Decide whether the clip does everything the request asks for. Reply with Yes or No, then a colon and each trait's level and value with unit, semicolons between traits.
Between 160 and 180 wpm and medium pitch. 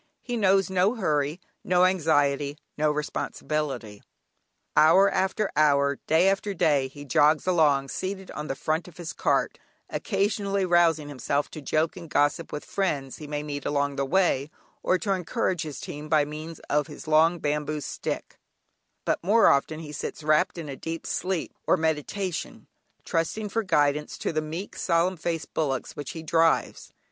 Yes: average, 165 wpm; medium, 155 Hz